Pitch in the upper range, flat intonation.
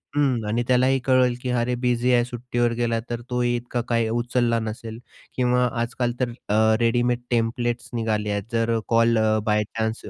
No: low, 120 Hz; narrow, 1.3 semitones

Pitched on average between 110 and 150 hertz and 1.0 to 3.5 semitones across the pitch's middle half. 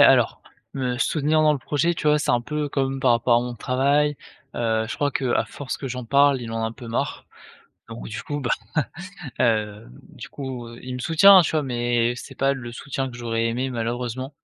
Yes: low, 130 Hz; average, 3.1 semitones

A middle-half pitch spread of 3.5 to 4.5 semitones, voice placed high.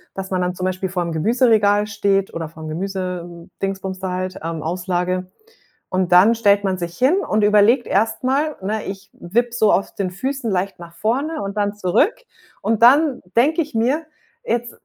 Yes: average, 4.2 semitones; high, 195 Hz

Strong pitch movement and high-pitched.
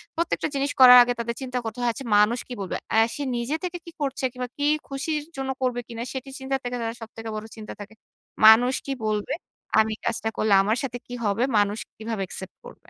No: average, 3.4 semitones; high, 240 Hz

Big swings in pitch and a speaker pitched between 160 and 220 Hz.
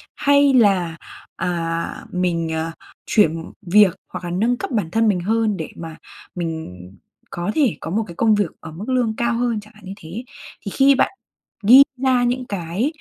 Yes: wide, 5.7 semitones; high, 205 Hz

